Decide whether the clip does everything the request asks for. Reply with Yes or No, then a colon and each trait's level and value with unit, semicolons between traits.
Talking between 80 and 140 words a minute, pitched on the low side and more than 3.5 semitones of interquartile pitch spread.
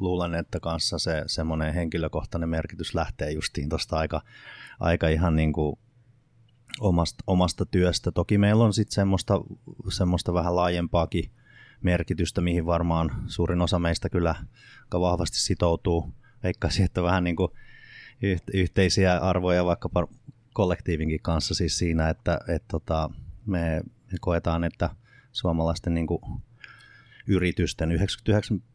No: average, 120 wpm; very low, 90 Hz; average, 2.8 semitones